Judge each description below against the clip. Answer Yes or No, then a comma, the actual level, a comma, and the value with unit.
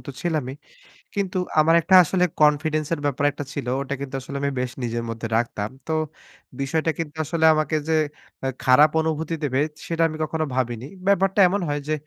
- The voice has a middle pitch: Yes, medium, 150 Hz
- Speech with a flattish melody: No, average, 3.2 semitones